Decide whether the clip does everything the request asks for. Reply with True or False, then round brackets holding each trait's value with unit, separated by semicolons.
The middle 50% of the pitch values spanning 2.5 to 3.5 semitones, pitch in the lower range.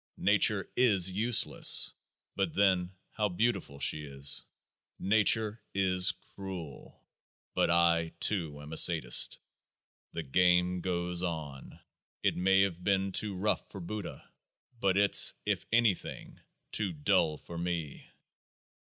True (2.9 semitones; 90 Hz)